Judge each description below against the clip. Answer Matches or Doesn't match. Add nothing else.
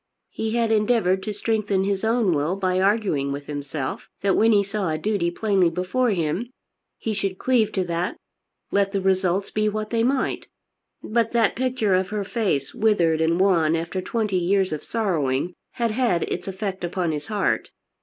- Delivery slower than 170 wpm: Doesn't match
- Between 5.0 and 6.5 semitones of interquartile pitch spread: Doesn't match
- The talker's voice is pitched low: Doesn't match